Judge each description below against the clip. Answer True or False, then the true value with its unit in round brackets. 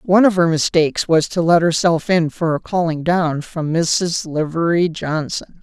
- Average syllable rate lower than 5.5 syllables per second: True (4.5 syllables/s)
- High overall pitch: False (165 Hz)